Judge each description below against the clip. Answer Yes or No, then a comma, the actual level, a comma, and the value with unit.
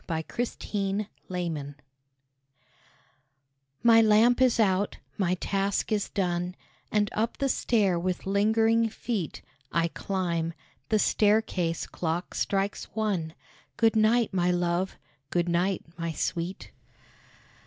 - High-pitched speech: Yes, high, 195 Hz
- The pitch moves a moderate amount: Yes, average, 3.8 semitones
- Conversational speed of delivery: No, slow, 115 wpm